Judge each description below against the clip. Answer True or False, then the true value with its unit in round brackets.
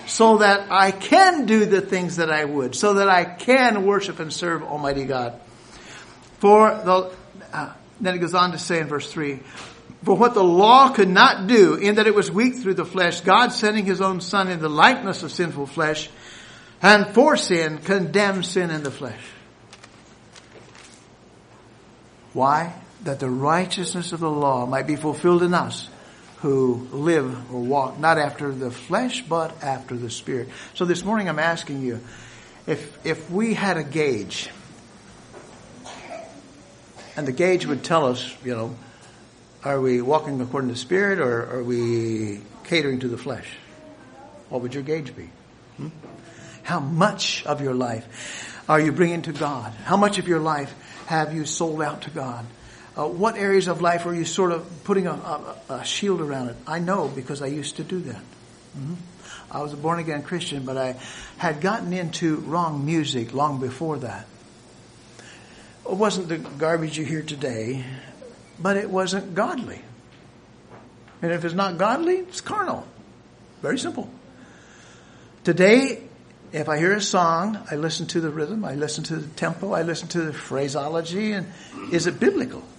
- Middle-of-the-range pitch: True (160 Hz)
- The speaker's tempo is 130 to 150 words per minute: False (170 wpm)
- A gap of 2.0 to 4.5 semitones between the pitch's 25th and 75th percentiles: False (5.4 semitones)